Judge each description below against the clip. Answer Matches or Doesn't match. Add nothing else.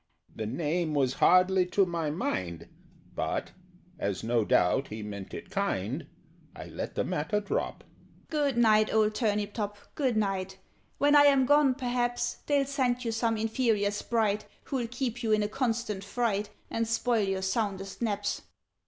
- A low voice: Doesn't match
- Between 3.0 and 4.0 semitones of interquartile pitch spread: Doesn't match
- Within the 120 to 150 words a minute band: Doesn't match